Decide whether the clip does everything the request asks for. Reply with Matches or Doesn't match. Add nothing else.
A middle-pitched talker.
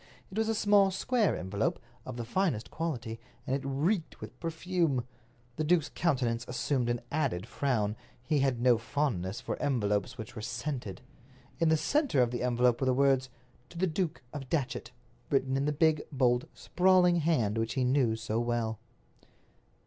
Doesn't match